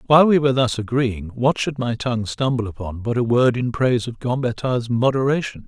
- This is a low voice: Yes, low, 125 Hz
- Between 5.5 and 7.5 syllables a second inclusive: Yes, 5.7 syllables/s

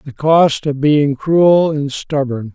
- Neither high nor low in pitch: Yes, medium, 145 Hz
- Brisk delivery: No, average, 165 wpm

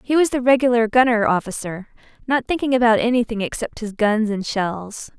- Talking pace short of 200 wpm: Yes, average, 175 wpm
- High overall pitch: Yes, high, 230 Hz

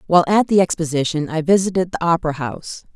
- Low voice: No, medium, 170 Hz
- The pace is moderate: Yes, average, 185 wpm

